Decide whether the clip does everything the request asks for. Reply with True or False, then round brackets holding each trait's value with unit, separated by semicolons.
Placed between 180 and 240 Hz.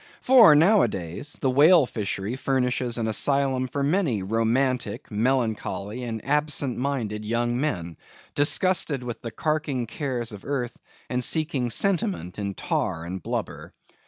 False (125 Hz)